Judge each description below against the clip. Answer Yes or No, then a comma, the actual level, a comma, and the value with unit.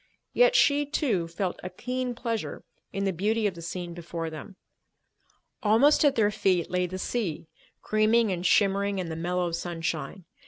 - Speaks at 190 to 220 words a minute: No, average, 165 wpm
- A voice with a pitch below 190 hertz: No, high, 195 Hz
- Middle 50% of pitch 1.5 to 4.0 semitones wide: No, average, 4.6 semitones